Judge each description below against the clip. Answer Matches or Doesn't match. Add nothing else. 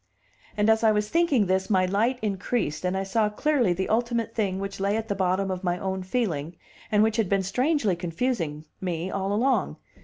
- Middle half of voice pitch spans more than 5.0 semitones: Doesn't match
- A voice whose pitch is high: Matches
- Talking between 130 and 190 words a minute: Doesn't match